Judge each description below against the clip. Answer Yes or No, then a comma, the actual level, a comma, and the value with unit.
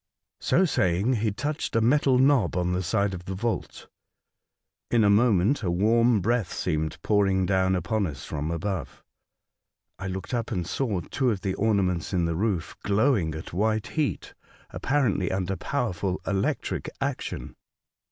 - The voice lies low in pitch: Yes, low, 100 Hz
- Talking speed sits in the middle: Yes, average, 155 wpm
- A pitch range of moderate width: Yes, average, 4.2 semitones